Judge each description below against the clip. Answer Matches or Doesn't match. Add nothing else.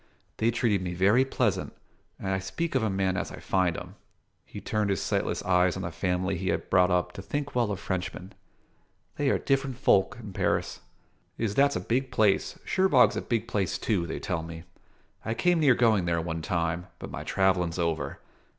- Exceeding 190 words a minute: Matches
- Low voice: Matches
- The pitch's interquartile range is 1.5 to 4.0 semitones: Doesn't match